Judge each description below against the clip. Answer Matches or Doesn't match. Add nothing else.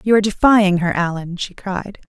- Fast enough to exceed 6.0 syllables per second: Doesn't match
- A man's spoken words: Doesn't match